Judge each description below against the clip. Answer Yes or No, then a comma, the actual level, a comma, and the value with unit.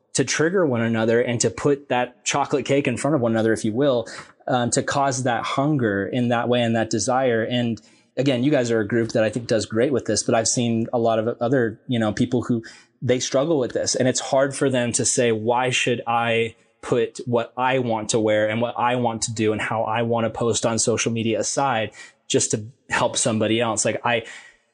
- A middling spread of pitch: No, narrow, 2.1 semitones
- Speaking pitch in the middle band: No, low, 120 Hz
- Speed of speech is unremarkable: No, fast, 235 wpm